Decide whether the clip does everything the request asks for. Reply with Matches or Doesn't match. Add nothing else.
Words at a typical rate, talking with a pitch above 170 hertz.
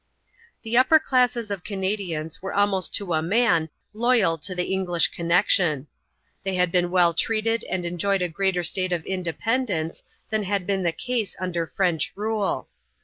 Matches